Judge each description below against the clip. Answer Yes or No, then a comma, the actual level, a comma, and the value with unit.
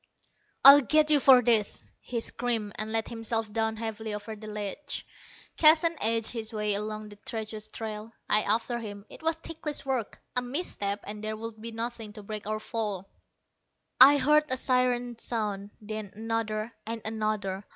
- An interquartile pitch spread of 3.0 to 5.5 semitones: No, narrow, 2.4 semitones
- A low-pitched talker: No, high, 220 Hz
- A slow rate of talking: No, average, 170 wpm